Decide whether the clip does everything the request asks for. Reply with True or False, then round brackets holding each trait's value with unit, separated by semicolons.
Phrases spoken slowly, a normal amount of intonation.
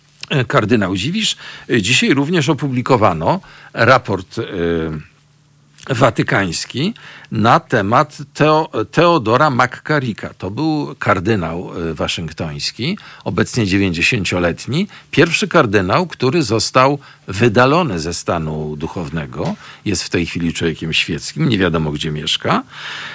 False (95 wpm; 8.9 semitones)